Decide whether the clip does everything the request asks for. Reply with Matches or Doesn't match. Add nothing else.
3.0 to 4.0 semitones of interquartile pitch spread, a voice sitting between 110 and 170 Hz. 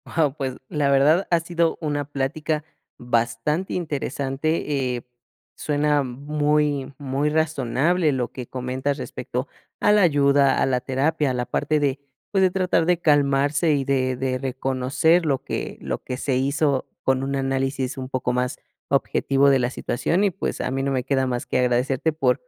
Doesn't match